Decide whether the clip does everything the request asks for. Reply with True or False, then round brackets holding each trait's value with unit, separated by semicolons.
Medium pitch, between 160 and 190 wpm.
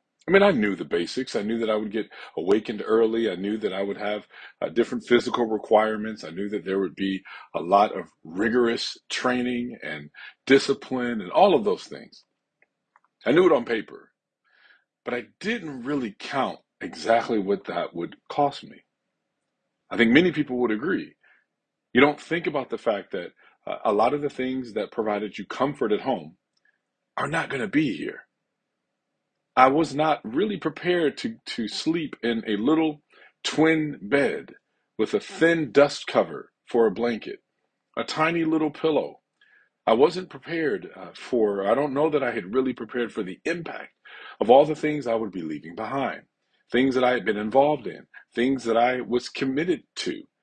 False (130 Hz; 180 wpm)